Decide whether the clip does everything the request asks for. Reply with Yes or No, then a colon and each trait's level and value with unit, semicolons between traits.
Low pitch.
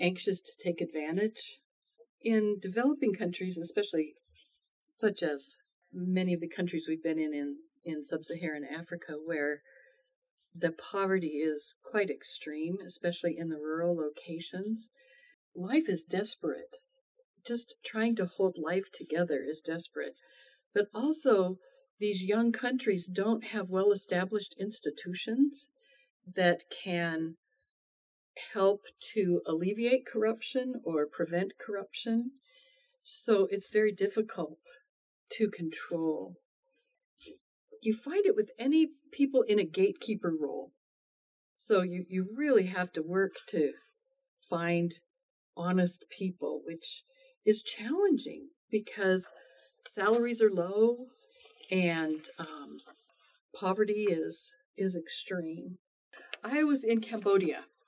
No: high, 200 Hz